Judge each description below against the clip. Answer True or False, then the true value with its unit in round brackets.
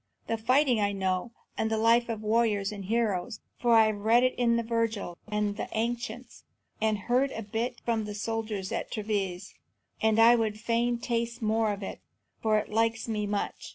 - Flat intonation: True (1.9 semitones)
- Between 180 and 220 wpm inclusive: True (190 wpm)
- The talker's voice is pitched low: False (220 Hz)